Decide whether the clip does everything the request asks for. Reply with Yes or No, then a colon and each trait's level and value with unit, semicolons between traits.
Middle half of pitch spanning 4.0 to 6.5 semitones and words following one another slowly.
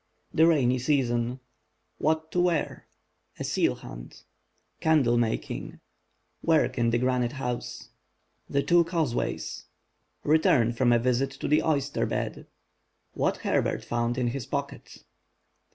Yes: average, 4.4 semitones; slow, 105 wpm